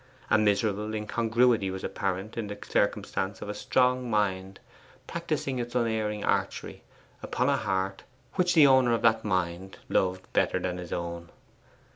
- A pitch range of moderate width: Yes, average, 4.0 semitones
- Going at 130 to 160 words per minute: Yes, average, 150 wpm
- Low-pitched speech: Yes, low, 105 Hz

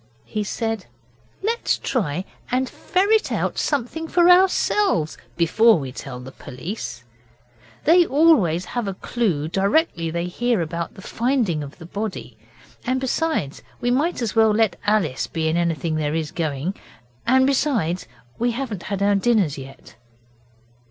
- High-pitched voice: Yes, high, 205 Hz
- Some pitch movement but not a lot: No, wide, 7.9 semitones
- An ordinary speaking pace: Yes, average, 145 wpm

